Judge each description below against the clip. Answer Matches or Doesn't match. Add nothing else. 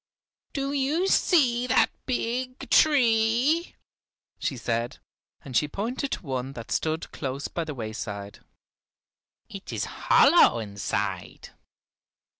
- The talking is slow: Matches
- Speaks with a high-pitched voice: Matches